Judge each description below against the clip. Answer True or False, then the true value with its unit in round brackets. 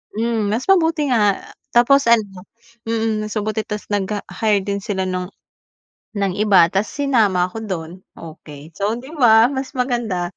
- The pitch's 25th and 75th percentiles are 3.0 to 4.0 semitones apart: True (3.6 semitones)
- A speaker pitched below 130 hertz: False (215 Hz)